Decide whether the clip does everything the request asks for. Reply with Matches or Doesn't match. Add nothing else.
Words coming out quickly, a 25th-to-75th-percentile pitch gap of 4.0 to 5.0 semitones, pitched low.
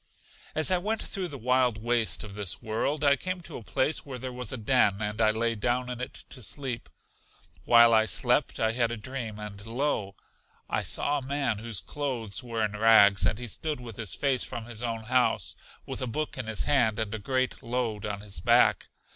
Doesn't match